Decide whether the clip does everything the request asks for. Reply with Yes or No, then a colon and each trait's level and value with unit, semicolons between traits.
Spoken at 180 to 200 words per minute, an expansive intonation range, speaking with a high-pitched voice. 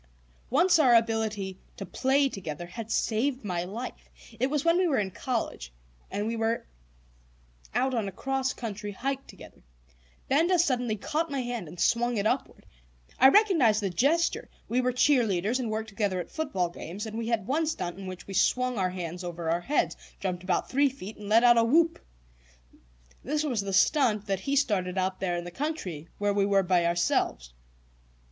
Yes: average, 185 wpm; wide, 5.9 semitones; high, 220 Hz